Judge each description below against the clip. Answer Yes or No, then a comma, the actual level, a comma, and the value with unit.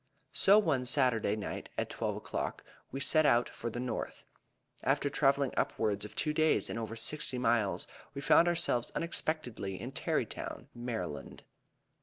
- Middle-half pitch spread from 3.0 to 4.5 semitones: No, average, 5.1 semitones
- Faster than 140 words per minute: Yes, average, 150 wpm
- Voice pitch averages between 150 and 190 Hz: No, low, 125 Hz